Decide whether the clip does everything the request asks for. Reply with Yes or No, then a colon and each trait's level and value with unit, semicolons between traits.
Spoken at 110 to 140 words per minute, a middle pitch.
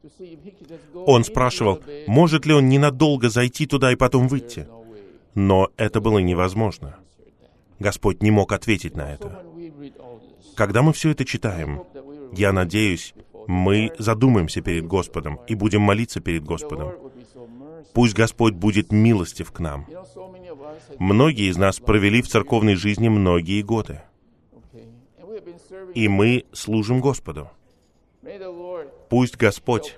No: average, 115 wpm; low, 115 Hz